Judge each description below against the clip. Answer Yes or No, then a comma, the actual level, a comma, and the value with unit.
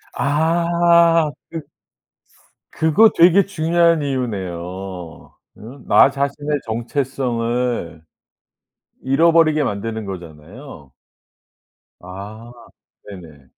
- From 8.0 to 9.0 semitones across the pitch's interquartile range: Yes, wide, 8.6 semitones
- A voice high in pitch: No, low, 130 Hz